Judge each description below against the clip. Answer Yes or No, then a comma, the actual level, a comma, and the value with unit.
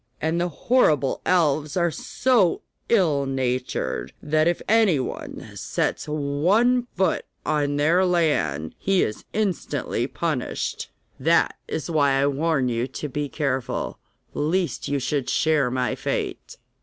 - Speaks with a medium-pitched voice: Yes, medium, 150 Hz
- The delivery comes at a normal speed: No, slow, 130 wpm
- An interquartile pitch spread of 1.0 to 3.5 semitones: No, average, 4.3 semitones